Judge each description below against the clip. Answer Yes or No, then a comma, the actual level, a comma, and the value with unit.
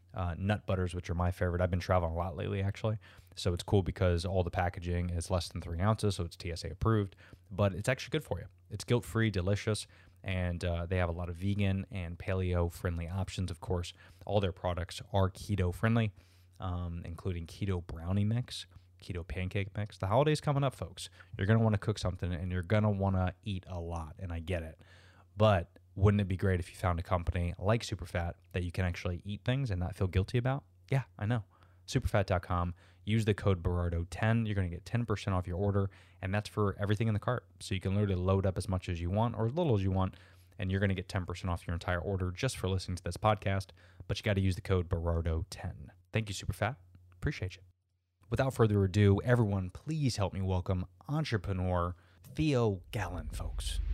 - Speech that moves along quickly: Yes, fast, 220 wpm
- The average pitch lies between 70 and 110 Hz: Yes, very low, 95 Hz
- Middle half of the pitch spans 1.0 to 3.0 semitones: Yes, average, 2.7 semitones